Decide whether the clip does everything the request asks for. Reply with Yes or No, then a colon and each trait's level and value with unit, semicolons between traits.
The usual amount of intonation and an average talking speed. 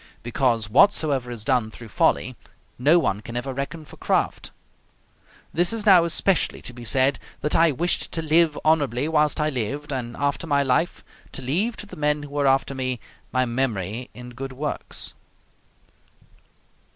Yes: average, 3.9 semitones; average, 165 wpm